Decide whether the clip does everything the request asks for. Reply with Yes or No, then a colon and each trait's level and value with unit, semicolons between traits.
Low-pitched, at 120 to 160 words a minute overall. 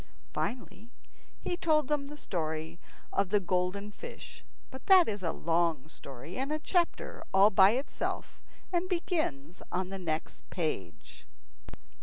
No: high, 195 Hz; average, 140 wpm